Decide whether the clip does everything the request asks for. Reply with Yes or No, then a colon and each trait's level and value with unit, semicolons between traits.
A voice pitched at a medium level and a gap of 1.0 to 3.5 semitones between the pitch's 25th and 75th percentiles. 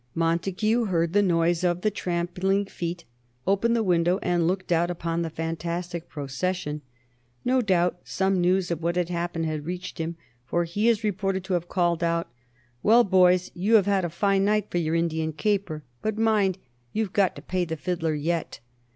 Yes: medium, 175 Hz; narrow, 2.5 semitones